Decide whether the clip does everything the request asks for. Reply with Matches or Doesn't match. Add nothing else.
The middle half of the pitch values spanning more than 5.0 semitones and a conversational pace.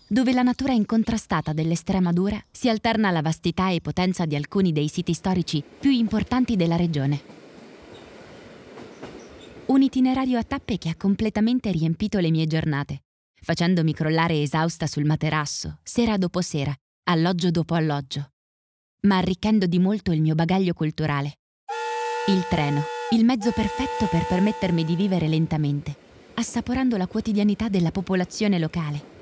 Matches